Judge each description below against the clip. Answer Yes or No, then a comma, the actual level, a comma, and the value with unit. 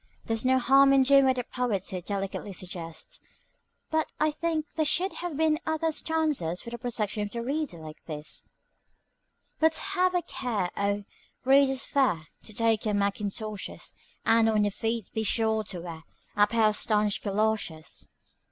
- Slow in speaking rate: No, average, 170 wpm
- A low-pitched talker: No, high, 225 Hz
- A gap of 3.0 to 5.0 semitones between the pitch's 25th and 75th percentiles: No, wide, 5.4 semitones